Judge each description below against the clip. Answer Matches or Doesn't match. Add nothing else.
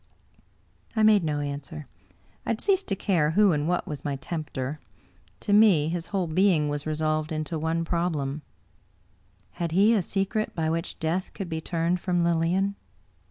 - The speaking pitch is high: Doesn't match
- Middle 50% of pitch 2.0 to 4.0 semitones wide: Matches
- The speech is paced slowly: Doesn't match